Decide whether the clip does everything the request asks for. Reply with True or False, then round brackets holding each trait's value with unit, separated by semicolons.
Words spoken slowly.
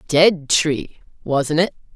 True (125 wpm)